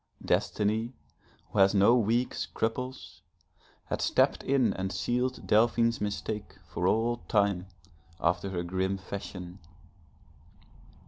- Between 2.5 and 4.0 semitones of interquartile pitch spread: Yes, average, 3.5 semitones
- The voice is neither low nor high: No, low, 105 Hz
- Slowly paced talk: Yes, slow, 110 wpm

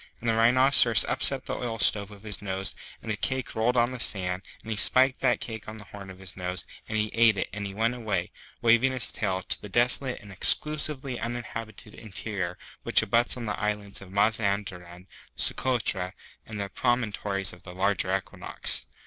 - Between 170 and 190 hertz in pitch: No, low, 105 Hz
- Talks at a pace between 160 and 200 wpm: Yes, average, 190 wpm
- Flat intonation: No, average, 3.3 semitones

